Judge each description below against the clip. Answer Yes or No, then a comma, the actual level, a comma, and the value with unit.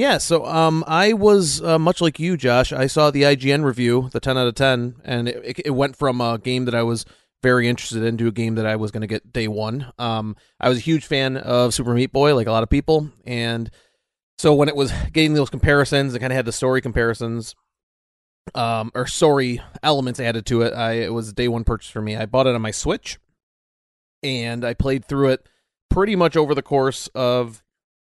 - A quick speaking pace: Yes, fast, 230 wpm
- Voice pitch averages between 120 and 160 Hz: Yes, low, 125 Hz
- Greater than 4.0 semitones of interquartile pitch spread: No, average, 3.5 semitones